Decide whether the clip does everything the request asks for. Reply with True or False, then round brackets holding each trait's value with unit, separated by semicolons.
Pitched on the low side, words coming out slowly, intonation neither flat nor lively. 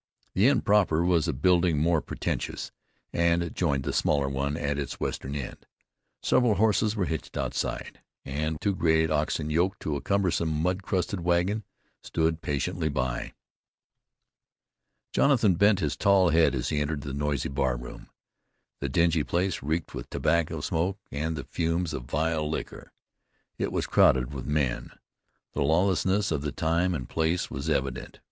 False (80 Hz; 160 wpm; 3.8 semitones)